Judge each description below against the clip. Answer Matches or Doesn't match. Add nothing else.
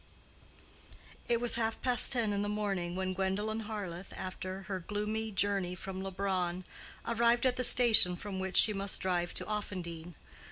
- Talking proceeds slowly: Doesn't match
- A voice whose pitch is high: Matches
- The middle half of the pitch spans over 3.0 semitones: Doesn't match